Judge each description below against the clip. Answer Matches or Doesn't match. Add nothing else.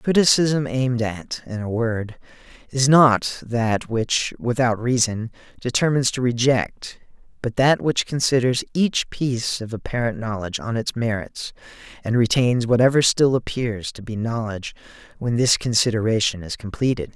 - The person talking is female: Doesn't match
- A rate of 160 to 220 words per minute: Doesn't match